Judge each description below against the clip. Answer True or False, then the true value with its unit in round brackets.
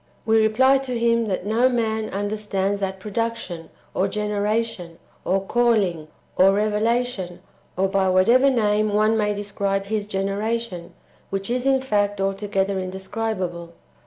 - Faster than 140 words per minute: False (135 wpm)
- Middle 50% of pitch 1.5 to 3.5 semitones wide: True (2.8 semitones)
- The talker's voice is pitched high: True (205 Hz)